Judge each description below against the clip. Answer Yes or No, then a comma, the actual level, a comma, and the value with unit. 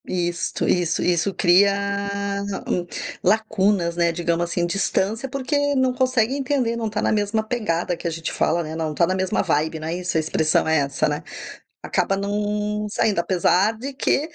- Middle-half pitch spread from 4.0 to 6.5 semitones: Yes, average, 4.4 semitones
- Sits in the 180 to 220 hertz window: Yes, high, 190 Hz